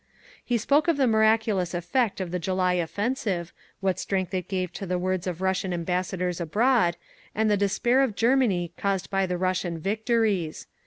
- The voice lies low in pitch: No, high, 190 Hz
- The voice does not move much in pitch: No, average, 3.5 semitones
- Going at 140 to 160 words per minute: No, average, 170 wpm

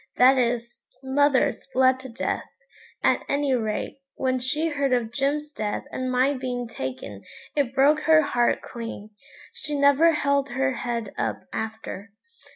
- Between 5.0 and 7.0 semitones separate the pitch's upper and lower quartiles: No, average, 3.1 semitones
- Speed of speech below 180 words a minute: Yes, average, 150 wpm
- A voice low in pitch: No, very high, 260 Hz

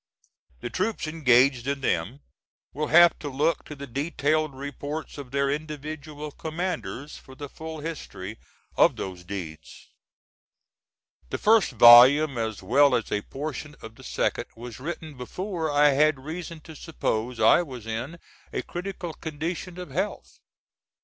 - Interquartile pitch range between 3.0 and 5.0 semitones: Yes, average, 4.3 semitones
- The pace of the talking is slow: No, average, 145 wpm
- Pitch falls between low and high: Yes, medium, 145 Hz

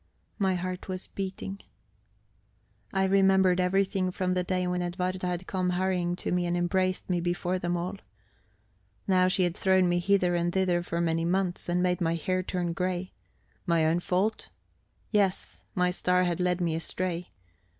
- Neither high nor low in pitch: Yes, medium, 180 Hz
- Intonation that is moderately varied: No, narrow, 1.2 semitones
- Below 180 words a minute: Yes, average, 170 wpm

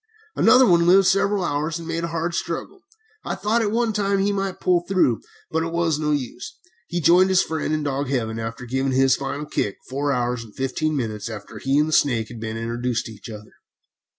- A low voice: No, medium, 150 Hz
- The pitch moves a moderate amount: No, wide, 6.2 semitones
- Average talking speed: No, fast, 220 wpm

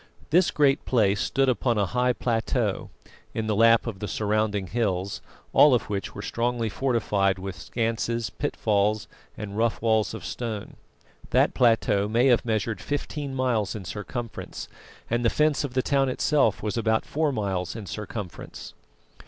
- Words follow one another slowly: No, average, 160 wpm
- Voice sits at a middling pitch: No, low, 115 Hz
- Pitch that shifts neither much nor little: Yes, average, 3.0 semitones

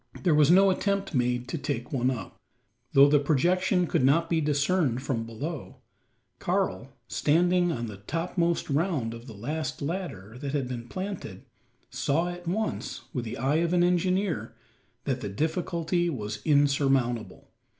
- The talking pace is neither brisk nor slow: Yes, average, 155 wpm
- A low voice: No, medium, 150 Hz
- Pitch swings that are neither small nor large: No, wide, 5.7 semitones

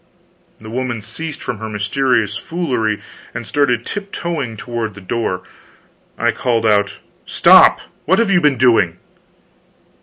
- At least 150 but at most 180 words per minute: No, average, 140 wpm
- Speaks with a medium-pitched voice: No, low, 120 Hz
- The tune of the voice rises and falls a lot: No, average, 4.8 semitones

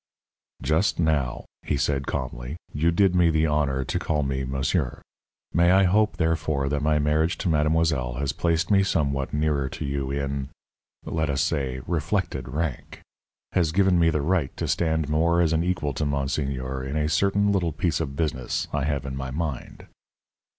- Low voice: Yes, very low, 75 Hz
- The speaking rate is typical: Yes, average, 180 wpm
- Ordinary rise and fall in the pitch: Yes, average, 3.4 semitones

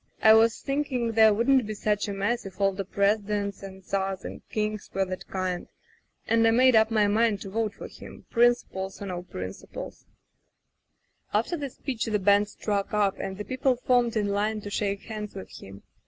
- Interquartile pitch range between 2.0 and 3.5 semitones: Yes, narrow, 2.6 semitones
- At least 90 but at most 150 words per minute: No, average, 195 wpm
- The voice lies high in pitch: Yes, high, 210 Hz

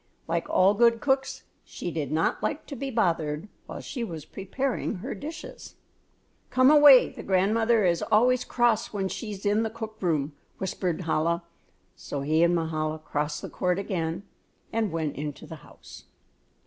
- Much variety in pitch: Yes, wide, 6.2 semitones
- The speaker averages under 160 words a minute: No, average, 165 wpm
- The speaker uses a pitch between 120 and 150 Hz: No, high, 190 Hz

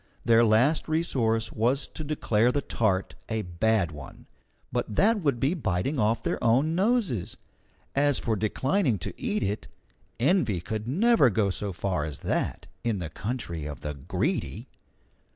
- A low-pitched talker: Yes, low, 115 Hz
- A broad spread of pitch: Yes, wide, 6.4 semitones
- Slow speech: No, average, 155 wpm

